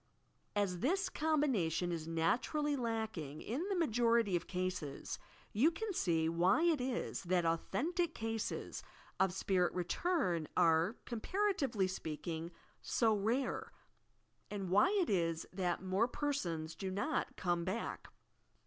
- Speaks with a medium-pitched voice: No, high, 200 Hz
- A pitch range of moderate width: No, wide, 7.7 semitones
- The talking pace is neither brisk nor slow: No, slow, 130 wpm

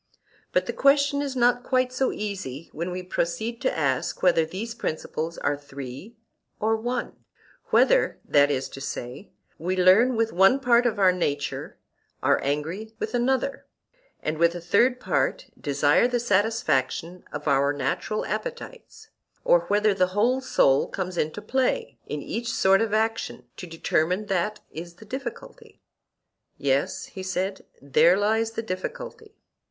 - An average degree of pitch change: No, wide, 6.8 semitones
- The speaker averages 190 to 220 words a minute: No, average, 150 wpm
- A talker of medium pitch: No, high, 195 Hz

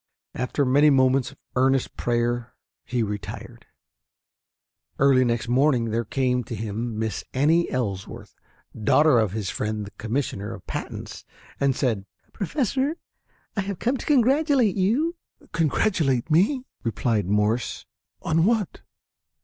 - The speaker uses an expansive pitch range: Yes, wide, 7.0 semitones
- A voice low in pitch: Yes, low, 130 Hz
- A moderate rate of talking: No, slow, 125 wpm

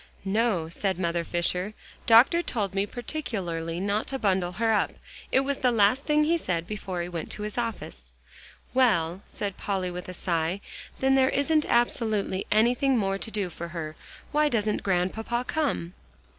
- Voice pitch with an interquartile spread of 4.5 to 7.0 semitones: Yes, average, 5.2 semitones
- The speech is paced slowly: No, average, 170 wpm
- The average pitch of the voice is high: Yes, high, 205 Hz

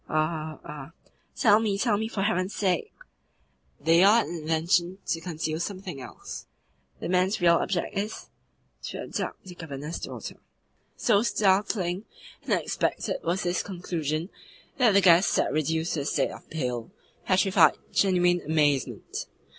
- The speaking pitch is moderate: Yes, medium, 175 Hz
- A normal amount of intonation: Yes, average, 3.7 semitones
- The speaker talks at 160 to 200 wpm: No, average, 150 wpm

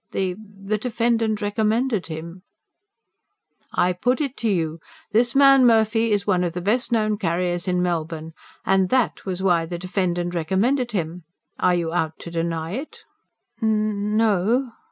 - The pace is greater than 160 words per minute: No, average, 155 wpm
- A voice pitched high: Yes, high, 195 Hz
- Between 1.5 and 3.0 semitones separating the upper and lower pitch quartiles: No, average, 4.3 semitones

